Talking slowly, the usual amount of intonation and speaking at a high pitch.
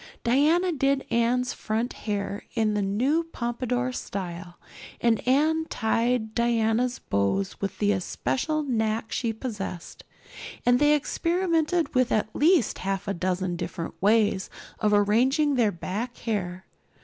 Yes: slow, 130 wpm; average, 4.6 semitones; high, 230 Hz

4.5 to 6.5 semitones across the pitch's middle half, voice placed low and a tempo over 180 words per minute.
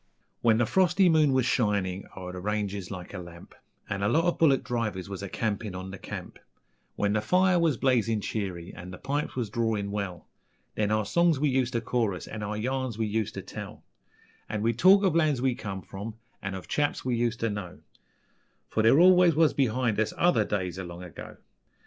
Yes: average, 5.0 semitones; low, 110 Hz; average, 200 wpm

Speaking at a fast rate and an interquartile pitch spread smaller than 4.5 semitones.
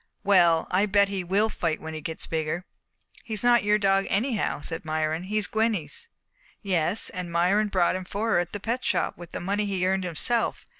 No: average, 195 wpm; average, 3.5 semitones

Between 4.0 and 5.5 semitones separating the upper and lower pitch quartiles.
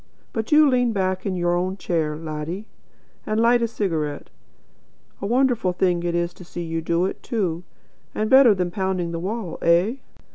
Yes: average, 4.4 semitones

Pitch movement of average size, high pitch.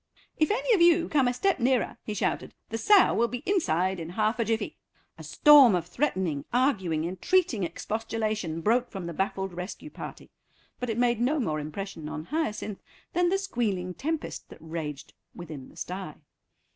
No: wide, 7.8 semitones; high, 215 Hz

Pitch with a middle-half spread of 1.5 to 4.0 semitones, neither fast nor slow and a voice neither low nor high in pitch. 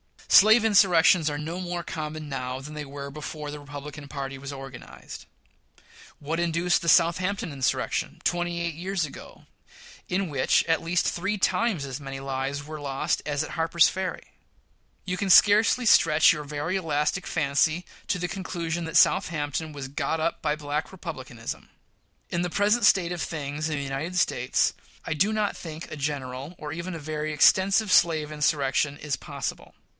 Yes: average, 3.4 semitones; average, 170 wpm; medium, 155 Hz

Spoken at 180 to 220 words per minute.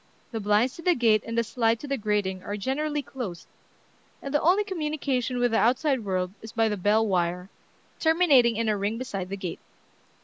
Yes: average, 200 wpm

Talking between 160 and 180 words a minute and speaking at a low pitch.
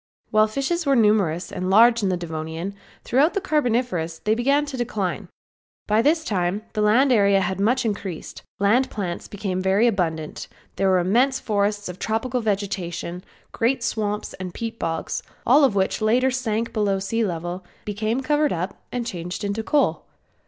No: average, 165 wpm; high, 210 Hz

